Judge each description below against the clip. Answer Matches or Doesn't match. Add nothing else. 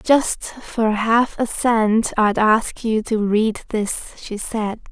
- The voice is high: Matches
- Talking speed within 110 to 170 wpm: Matches